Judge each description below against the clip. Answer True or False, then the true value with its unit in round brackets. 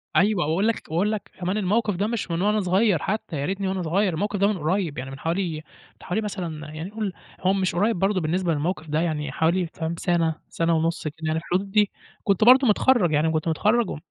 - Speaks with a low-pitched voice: False (180 Hz)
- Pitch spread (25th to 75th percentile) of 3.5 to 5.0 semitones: True (4.2 semitones)